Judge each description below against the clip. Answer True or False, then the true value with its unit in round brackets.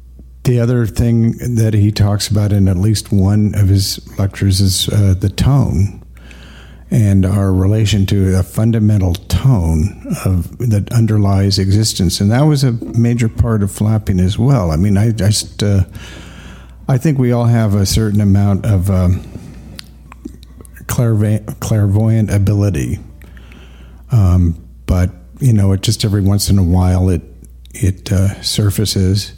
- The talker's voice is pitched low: True (100 Hz)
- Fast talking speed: False (150 wpm)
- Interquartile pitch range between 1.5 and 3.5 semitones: True (3.1 semitones)